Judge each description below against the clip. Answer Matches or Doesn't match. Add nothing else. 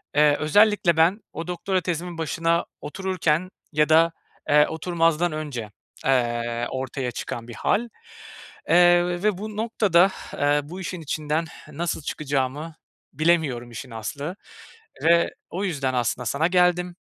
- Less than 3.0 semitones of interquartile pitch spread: Doesn't match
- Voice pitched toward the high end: Doesn't match